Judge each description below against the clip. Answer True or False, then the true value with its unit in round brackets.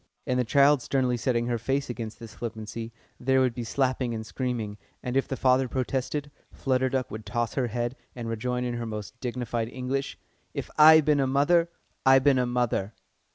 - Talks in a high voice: False (125 Hz)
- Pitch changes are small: True (2.2 semitones)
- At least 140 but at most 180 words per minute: False (200 wpm)